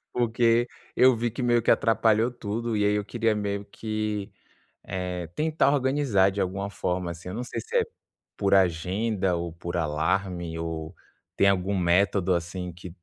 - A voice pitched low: Yes, low, 100 Hz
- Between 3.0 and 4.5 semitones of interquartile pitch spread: Yes, average, 4.2 semitones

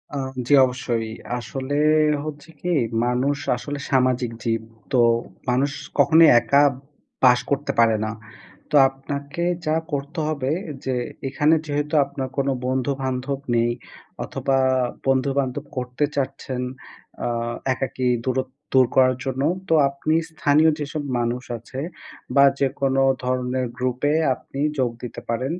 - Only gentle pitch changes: Yes, narrow, 2.1 semitones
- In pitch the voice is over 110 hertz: Yes, low, 135 Hz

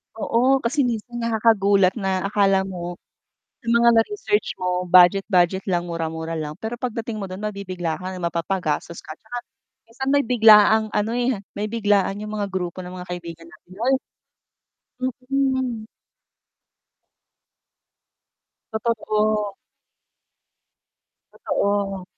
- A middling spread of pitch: Yes, average, 4.0 semitones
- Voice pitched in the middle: No, high, 205 Hz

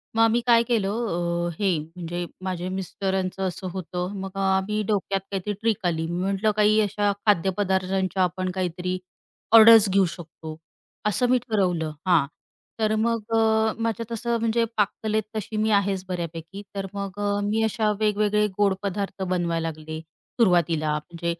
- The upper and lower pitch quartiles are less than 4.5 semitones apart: Yes, average, 3.2 semitones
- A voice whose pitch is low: No, high, 195 Hz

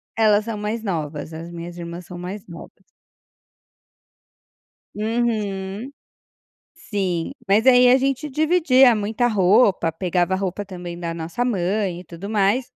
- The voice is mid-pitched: No, high, 200 Hz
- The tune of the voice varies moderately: Yes, average, 4.6 semitones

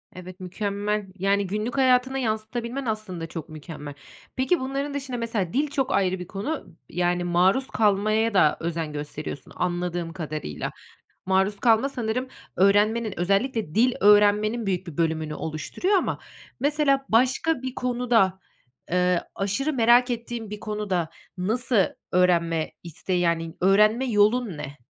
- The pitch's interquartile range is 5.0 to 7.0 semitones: Yes, wide, 5.4 semitones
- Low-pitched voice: No, high, 205 Hz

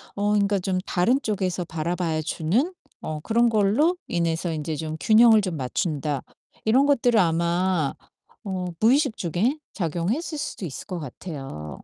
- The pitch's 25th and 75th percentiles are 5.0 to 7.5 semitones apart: Yes, wide, 5.5 semitones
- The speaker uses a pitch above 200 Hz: No, medium, 185 Hz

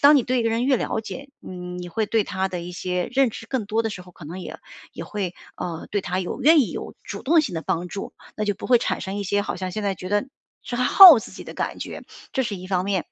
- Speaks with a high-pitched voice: Yes, high, 205 Hz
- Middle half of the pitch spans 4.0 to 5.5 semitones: Yes, average, 4.9 semitones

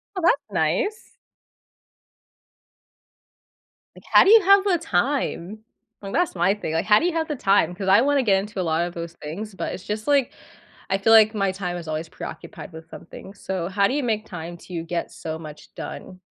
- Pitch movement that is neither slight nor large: No, wide, 7.1 semitones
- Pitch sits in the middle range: No, high, 195 Hz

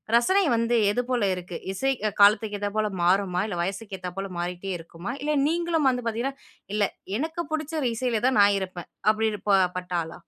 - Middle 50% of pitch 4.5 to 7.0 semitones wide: Yes, average, 5.2 semitones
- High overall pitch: Yes, high, 215 Hz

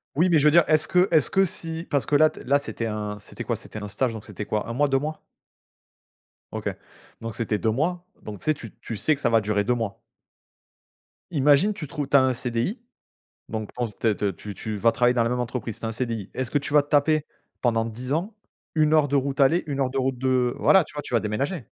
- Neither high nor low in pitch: No, low, 130 Hz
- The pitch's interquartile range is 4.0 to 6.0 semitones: Yes, average, 5.0 semitones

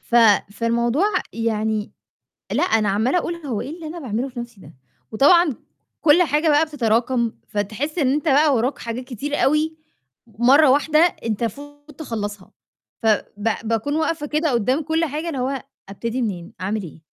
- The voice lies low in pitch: No, very high, 260 Hz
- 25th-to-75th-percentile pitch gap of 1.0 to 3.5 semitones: No, wide, 5.4 semitones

